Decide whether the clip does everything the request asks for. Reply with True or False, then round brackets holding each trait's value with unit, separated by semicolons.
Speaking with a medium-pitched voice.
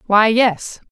False (210 Hz)